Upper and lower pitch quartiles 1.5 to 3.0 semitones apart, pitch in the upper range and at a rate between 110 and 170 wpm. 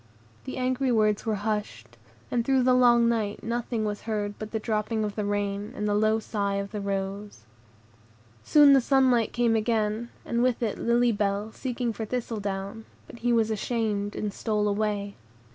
No: narrow, 2.4 semitones; high, 215 Hz; average, 180 wpm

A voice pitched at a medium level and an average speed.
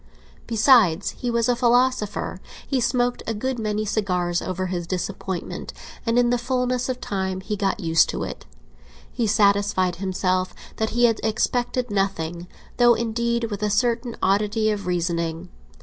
No: high, 210 Hz; average, 155 wpm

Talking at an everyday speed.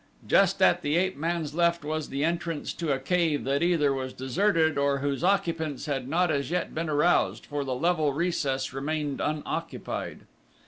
Yes: average, 175 wpm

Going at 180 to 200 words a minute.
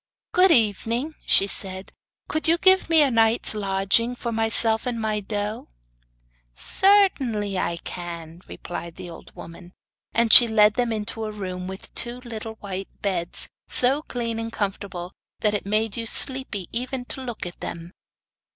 No: average, 160 wpm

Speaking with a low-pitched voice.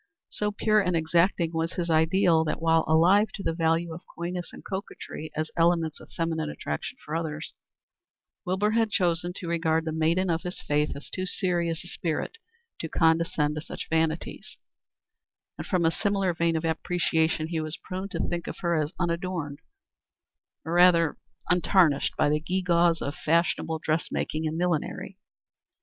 No: medium, 165 Hz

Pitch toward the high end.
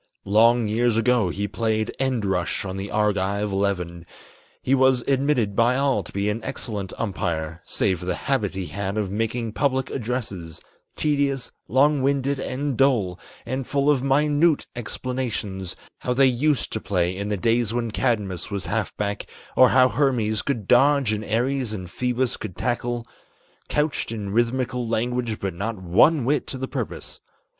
No: low, 115 Hz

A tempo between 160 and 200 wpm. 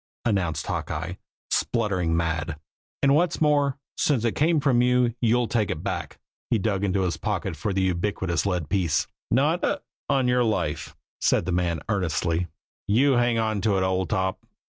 Yes: average, 170 wpm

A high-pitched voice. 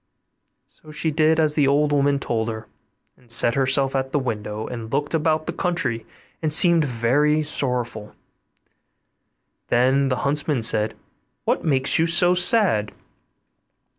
No: medium, 140 Hz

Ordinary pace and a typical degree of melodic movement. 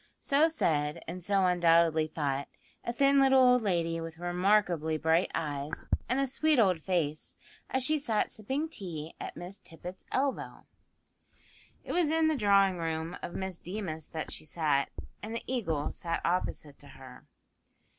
No: average, 160 wpm; wide, 6.6 semitones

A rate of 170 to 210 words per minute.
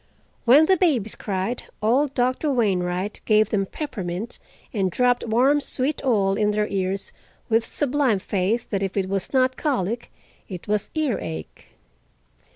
No: average, 145 wpm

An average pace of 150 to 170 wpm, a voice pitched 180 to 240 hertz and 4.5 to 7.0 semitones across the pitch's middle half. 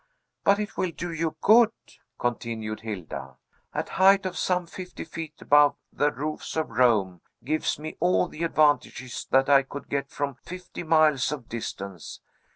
No: average, 160 wpm; medium, 150 Hz; wide, 5.6 semitones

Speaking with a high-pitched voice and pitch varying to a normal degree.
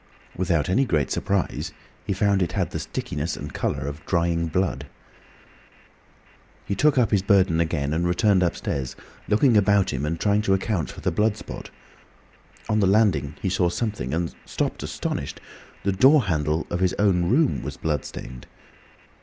No: very low, 95 Hz; average, 3.9 semitones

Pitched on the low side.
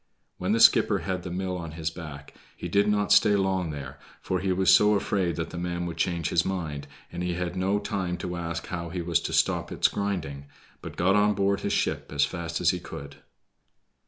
Yes: very low, 90 Hz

